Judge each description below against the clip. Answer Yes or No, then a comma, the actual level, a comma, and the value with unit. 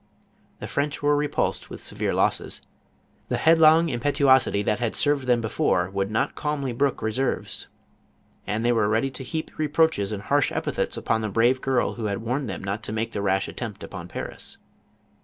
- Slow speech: No, average, 185 wpm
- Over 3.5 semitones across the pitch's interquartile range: Yes, average, 5.0 semitones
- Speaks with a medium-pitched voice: No, low, 120 Hz